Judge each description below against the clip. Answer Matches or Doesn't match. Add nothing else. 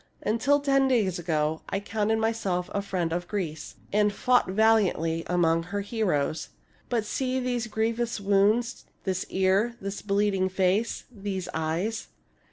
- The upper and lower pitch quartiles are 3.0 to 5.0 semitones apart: Matches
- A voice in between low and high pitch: Doesn't match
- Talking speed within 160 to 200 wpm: Doesn't match